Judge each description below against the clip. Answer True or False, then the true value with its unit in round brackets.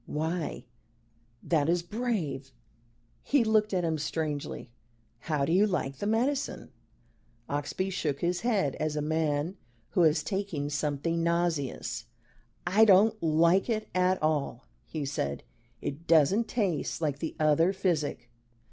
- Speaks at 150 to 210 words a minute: False (140 wpm)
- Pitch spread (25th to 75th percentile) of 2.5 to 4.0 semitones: False (4.6 semitones)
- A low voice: False (165 Hz)